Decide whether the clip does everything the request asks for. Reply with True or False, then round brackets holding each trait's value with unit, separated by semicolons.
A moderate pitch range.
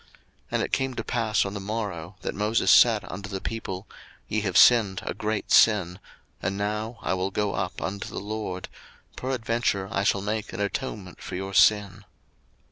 False (2.3 semitones)